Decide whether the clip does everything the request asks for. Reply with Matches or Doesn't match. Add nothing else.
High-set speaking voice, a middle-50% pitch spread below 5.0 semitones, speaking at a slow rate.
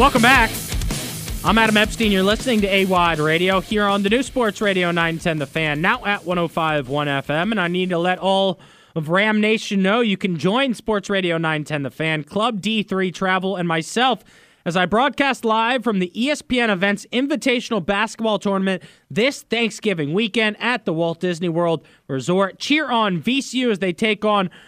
Doesn't match